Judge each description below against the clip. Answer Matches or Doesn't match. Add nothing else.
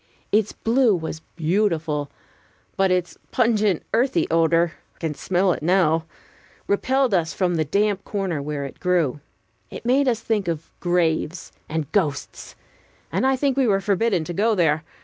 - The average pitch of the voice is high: Doesn't match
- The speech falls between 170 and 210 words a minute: Doesn't match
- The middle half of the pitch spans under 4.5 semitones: Doesn't match